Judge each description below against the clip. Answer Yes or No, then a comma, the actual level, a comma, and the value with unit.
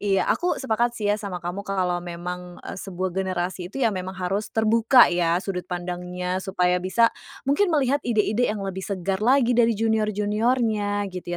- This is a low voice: No, high, 200 Hz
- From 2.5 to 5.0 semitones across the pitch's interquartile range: Yes, average, 3.8 semitones